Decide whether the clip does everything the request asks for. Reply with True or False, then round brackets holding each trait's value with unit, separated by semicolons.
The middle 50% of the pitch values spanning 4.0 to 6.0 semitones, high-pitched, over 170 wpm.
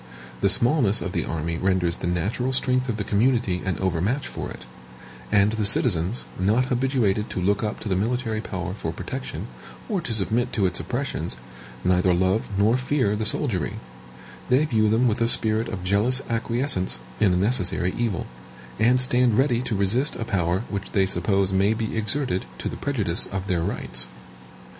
False (4.7 semitones; 105 Hz; 180 wpm)